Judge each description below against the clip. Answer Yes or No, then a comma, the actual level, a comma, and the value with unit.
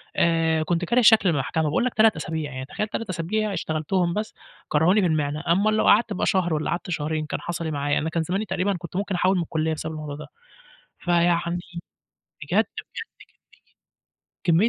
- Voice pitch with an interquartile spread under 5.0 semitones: Yes, average, 3.5 semitones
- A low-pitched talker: No, medium, 170 Hz